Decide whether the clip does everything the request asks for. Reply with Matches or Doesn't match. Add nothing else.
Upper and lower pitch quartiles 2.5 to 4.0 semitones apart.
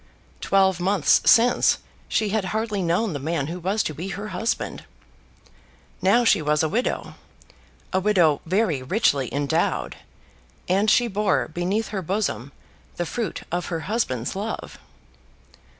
Doesn't match